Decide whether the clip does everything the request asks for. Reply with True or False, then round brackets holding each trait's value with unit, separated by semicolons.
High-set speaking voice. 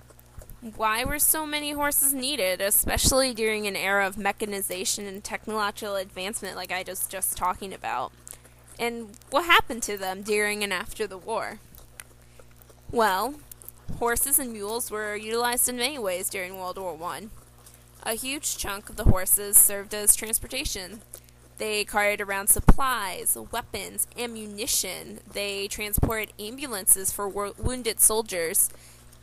True (205 Hz)